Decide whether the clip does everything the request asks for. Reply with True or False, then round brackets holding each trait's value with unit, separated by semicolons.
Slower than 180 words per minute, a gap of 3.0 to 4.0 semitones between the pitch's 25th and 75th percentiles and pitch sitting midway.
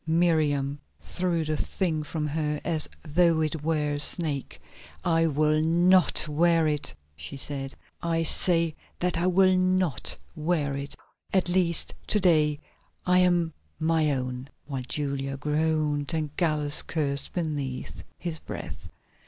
False (135 wpm; 2.6 semitones; 155 Hz)